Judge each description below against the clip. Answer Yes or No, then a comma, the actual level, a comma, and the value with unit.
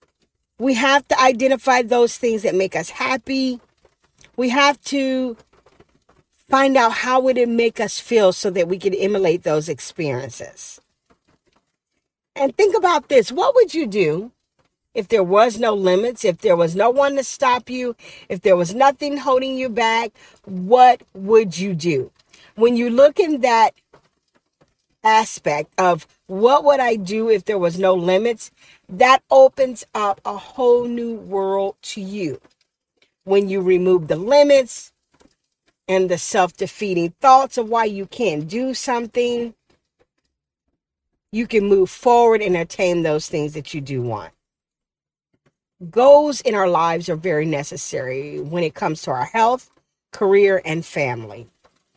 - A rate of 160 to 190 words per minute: No, average, 150 wpm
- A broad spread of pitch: Yes, wide, 5.8 semitones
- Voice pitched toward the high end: Yes, high, 220 Hz